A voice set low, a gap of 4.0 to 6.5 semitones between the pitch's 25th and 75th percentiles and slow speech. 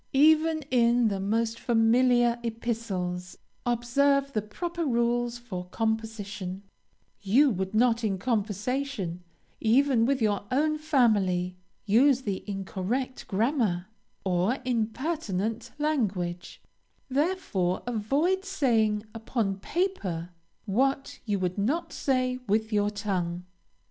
No: high, 225 Hz; average, 4.8 semitones; slow, 105 wpm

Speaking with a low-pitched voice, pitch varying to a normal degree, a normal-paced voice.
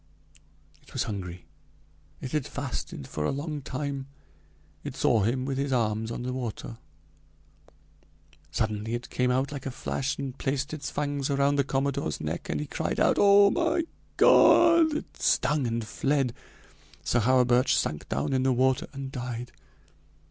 Yes: low, 130 Hz; average, 3.1 semitones; average, 160 wpm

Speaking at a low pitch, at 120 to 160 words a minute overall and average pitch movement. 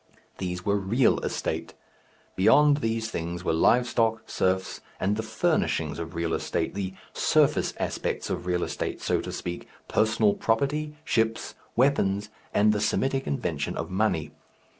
Yes: low, 105 Hz; average, 145 wpm; average, 4.2 semitones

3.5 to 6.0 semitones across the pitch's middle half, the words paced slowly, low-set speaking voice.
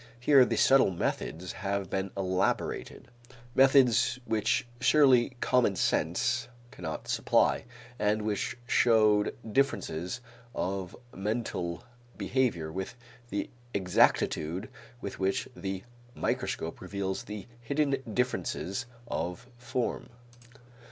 Yes: average, 4.9 semitones; slow, 95 wpm; low, 105 Hz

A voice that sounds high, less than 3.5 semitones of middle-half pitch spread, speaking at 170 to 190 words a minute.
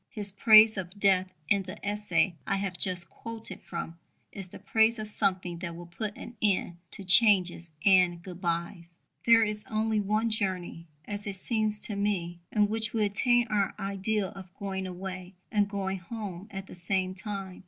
Yes: high, 195 Hz; narrow, 2.5 semitones; average, 175 wpm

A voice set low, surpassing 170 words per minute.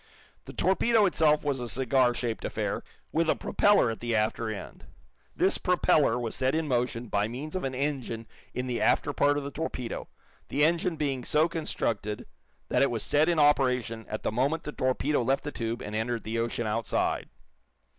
Yes: low, 130 Hz; average, 190 wpm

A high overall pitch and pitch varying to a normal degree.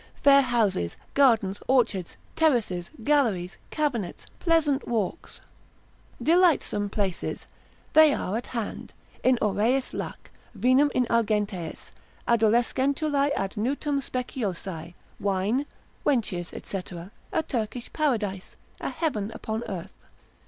No: high, 230 Hz; wide, 6.0 semitones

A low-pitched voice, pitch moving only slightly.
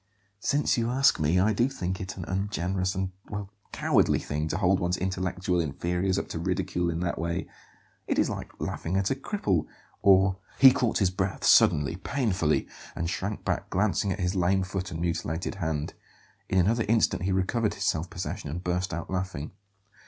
Yes: very low, 95 Hz; narrow, 2.3 semitones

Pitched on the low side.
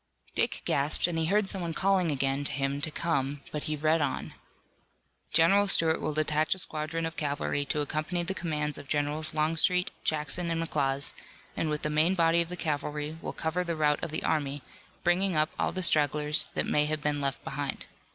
No: medium, 155 Hz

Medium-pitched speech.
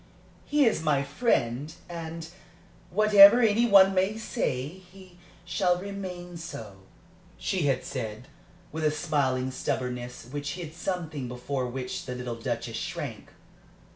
Yes: medium, 160 Hz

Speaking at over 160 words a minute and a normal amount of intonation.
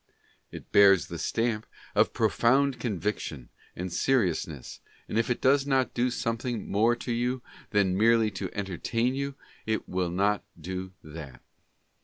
No: average, 145 wpm; average, 4.7 semitones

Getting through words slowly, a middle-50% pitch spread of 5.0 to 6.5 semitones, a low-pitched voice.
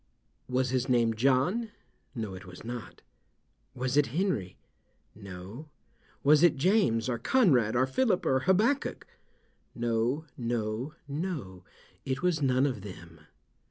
Yes: slow, 125 wpm; average, 5.3 semitones; low, 130 Hz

